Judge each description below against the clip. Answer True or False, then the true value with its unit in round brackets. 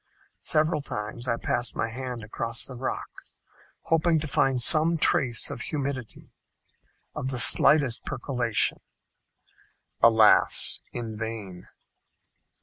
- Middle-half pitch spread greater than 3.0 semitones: True (3.6 semitones)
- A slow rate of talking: True (110 wpm)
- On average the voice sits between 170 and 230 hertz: False (125 Hz)